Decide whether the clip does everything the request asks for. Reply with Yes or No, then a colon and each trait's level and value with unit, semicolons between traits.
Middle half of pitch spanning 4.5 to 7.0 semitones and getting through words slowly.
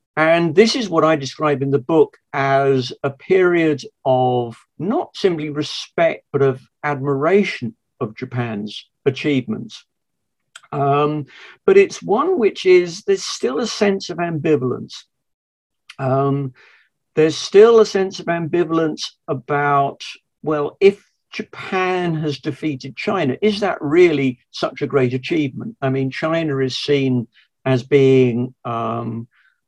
Yes: average, 5.3 semitones; slow, 125 wpm